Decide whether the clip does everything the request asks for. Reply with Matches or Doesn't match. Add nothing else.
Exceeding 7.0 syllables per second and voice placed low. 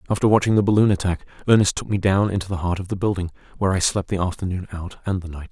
Matches